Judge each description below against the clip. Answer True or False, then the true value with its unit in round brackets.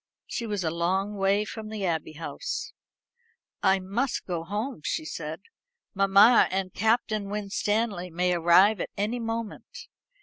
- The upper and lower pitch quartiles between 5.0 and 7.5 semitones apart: False (3.2 semitones)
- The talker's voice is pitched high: True (195 Hz)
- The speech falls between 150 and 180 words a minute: False (140 wpm)